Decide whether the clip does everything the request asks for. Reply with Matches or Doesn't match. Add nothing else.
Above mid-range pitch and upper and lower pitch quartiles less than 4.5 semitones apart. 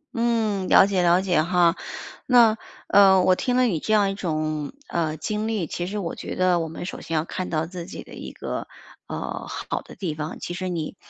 Doesn't match